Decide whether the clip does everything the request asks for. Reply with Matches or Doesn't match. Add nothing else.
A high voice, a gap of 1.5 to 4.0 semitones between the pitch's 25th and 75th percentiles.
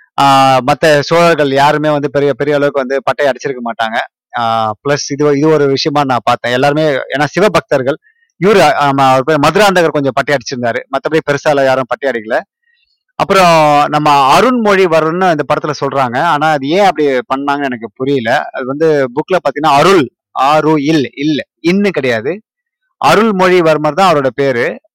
Doesn't match